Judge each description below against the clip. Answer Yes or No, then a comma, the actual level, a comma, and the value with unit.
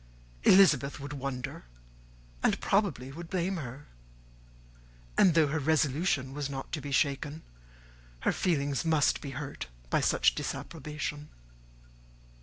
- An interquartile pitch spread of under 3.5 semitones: Yes, average, 2.7 semitones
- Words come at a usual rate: No, slow, 125 wpm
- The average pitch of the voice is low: No, medium, 145 Hz